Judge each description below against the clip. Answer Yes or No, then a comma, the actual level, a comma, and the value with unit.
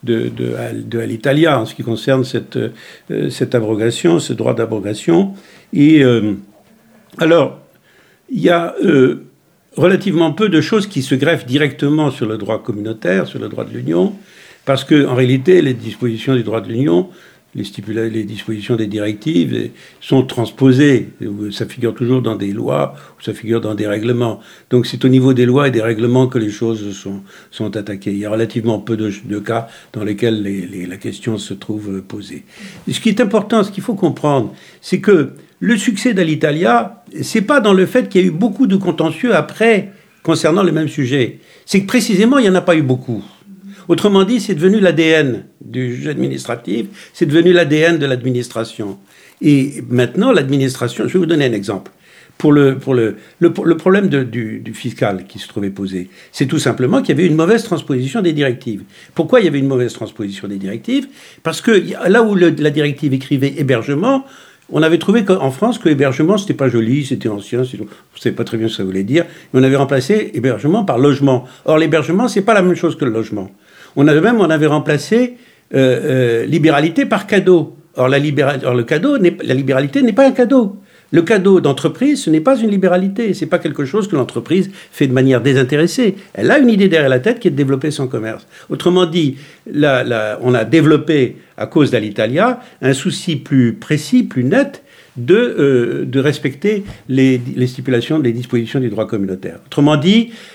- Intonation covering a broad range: Yes, wide, 7.4 semitones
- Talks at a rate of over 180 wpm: Yes, average, 195 wpm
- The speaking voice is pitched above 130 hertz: Yes, medium, 140 Hz